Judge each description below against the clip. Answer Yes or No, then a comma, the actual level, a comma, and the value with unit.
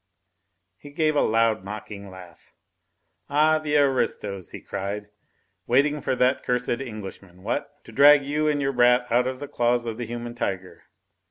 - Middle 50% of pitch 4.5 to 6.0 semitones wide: Yes, average, 5.1 semitones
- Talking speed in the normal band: Yes, average, 165 wpm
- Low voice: Yes, low, 120 Hz